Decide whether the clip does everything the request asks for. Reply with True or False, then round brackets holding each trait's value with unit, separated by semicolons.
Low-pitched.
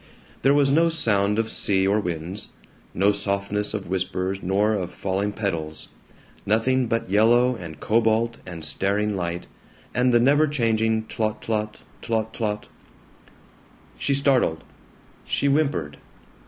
True (105 Hz)